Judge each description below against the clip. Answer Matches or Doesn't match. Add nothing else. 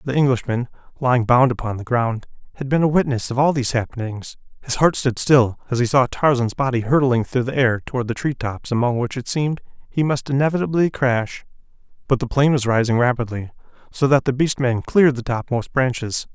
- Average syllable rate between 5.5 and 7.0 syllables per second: Matches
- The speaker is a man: Matches